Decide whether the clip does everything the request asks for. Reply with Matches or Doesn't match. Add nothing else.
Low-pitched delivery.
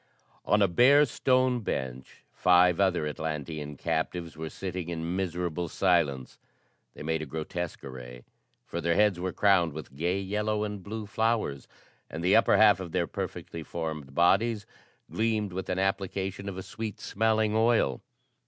Matches